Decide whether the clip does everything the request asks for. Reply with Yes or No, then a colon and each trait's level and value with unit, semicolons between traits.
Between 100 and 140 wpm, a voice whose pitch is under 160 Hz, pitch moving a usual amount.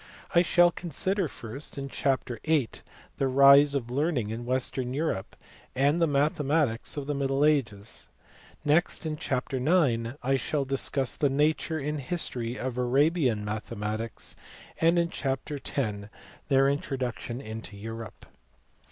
Yes: slow, 135 wpm; low, 135 Hz; average, 3.7 semitones